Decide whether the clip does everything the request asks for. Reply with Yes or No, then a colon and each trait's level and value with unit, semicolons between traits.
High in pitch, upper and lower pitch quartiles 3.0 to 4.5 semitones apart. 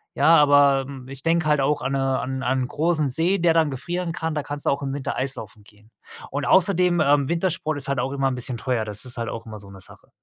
No: medium, 140 Hz; average, 3.9 semitones